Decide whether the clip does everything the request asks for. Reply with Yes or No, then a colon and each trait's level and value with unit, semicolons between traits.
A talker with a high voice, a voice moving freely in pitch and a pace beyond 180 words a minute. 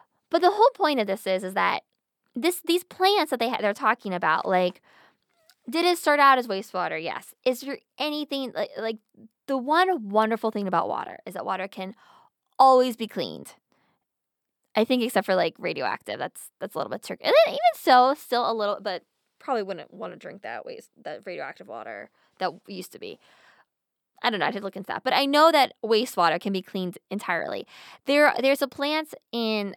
Yes: high, 240 Hz; wide, 6.6 semitones; average, 200 wpm